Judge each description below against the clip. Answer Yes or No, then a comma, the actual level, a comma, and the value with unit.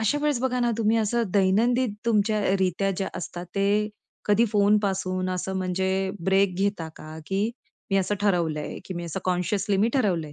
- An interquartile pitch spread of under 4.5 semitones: Yes, narrow, 2.4 semitones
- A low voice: No, high, 195 Hz